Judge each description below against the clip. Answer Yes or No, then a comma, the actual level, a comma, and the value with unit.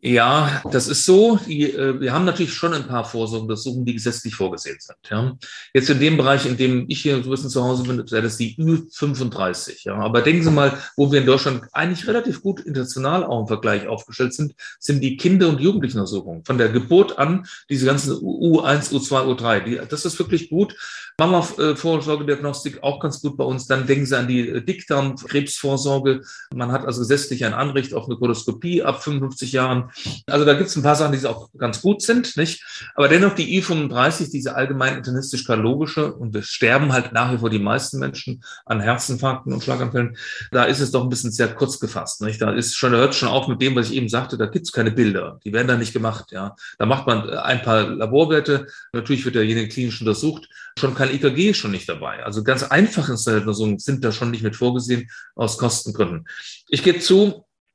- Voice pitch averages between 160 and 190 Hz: No, low, 135 Hz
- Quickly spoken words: Yes, fast, 205 wpm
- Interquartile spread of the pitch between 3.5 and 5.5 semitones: Yes, average, 3.8 semitones